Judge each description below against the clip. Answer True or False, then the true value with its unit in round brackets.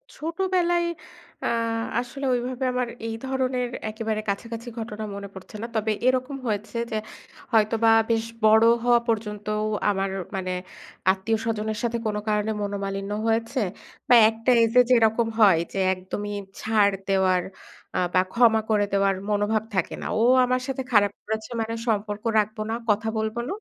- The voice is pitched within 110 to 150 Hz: False (220 Hz)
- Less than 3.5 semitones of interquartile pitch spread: True (2.4 semitones)